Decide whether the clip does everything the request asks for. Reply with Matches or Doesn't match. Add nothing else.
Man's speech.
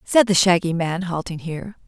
Doesn't match